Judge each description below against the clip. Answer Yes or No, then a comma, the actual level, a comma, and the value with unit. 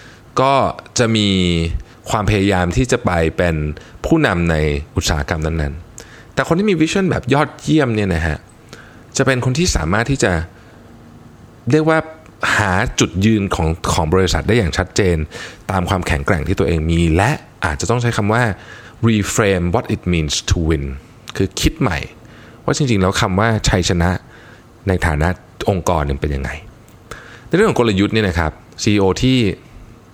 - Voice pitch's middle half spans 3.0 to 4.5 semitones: No, average, 5.2 semitones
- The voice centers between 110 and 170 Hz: No, low, 100 Hz